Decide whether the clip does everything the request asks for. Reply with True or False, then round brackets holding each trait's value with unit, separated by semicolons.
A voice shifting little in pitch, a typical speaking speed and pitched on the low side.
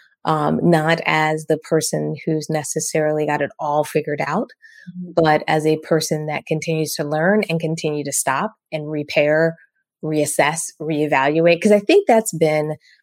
False (1.5 semitones; 150 wpm; 155 Hz)